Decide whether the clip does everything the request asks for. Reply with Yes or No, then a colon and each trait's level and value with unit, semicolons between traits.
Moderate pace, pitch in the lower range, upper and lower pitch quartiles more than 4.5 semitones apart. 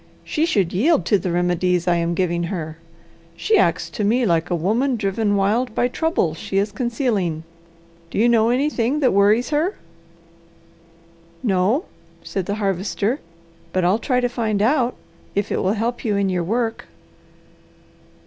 No: average, 160 wpm; high, 210 Hz; average, 5.0 semitones